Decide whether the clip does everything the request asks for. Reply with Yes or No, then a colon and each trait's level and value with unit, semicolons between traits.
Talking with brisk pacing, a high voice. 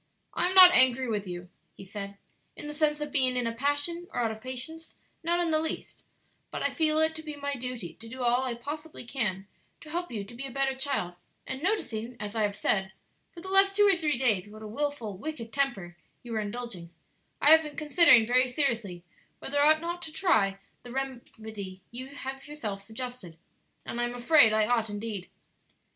Yes: fast, 215 wpm; very high, 255 Hz